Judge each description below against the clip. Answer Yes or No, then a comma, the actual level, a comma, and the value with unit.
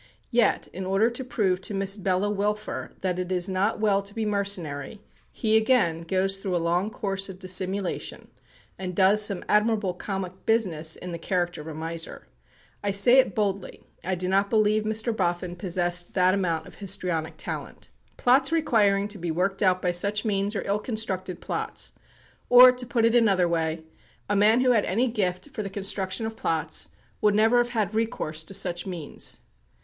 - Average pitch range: Yes, average, 3.1 semitones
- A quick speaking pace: No, average, 185 wpm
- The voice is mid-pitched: No, high, 195 Hz